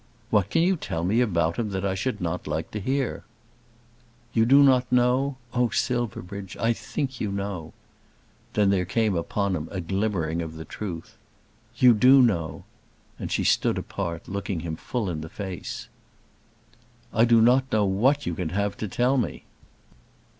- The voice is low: Yes, low, 100 Hz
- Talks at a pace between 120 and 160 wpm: No, average, 170 wpm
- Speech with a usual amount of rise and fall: No, wide, 5.7 semitones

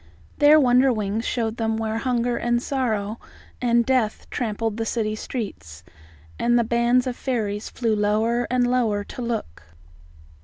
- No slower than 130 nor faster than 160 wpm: Yes, average, 145 wpm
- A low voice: No, high, 235 Hz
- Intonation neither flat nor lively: No, narrow, 2.2 semitones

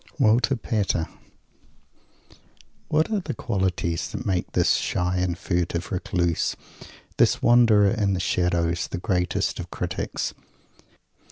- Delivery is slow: Yes, slow, 115 wpm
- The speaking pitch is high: No, very low, 95 Hz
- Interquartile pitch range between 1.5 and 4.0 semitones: Yes, average, 3.6 semitones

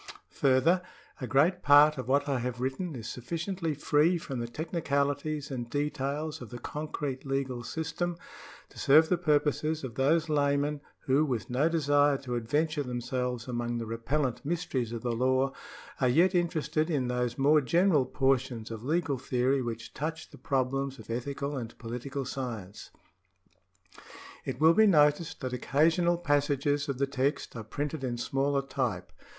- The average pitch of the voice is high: No, medium, 140 Hz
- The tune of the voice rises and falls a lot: No, average, 3.4 semitones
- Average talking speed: Yes, average, 160 wpm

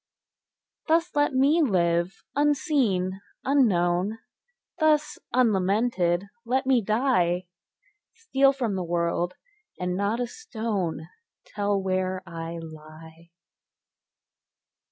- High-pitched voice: Yes, high, 200 Hz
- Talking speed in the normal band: No, slow, 95 wpm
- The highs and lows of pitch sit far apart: Yes, wide, 7.2 semitones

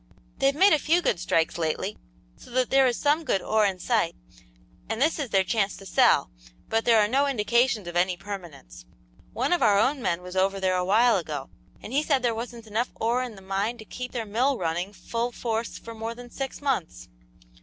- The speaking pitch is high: Yes, high, 225 Hz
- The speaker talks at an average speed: No, fast, 220 wpm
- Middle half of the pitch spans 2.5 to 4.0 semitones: No, average, 4.8 semitones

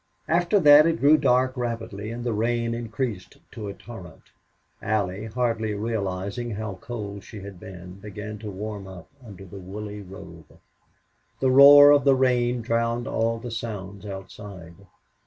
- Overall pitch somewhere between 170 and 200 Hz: No, low, 110 Hz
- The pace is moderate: Yes, average, 155 wpm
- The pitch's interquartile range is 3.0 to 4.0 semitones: Yes, average, 3.4 semitones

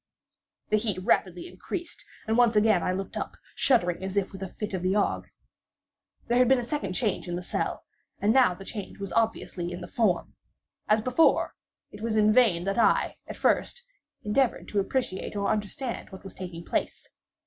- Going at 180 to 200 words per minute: Yes, average, 185 wpm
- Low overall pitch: No, high, 210 Hz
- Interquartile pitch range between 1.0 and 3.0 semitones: No, average, 3.8 semitones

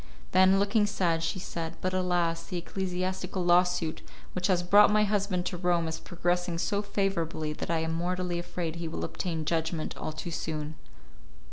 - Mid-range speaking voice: Yes, medium, 175 Hz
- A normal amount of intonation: No, narrow, 2.0 semitones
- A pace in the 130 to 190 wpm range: Yes, average, 170 wpm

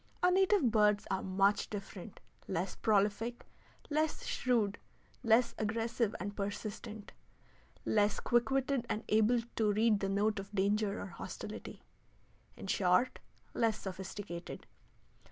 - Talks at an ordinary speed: No, slow, 120 wpm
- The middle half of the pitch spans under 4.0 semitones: Yes, average, 2.7 semitones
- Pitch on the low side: No, high, 210 Hz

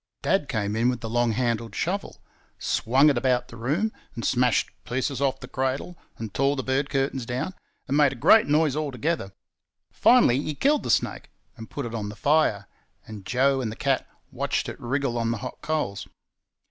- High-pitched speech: No, low, 130 Hz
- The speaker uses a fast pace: No, average, 195 wpm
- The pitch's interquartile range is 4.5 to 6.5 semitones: No, average, 3.6 semitones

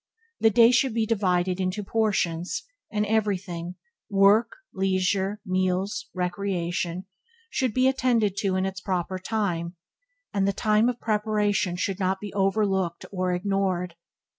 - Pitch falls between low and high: No, high, 195 Hz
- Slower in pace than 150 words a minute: Yes, average, 140 wpm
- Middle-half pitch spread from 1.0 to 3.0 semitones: Yes, narrow, 2.6 semitones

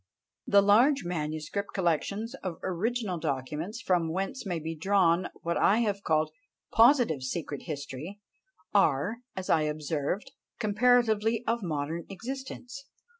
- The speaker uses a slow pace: Yes, slow, 125 wpm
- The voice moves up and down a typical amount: No, wide, 5.8 semitones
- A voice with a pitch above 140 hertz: Yes, medium, 185 Hz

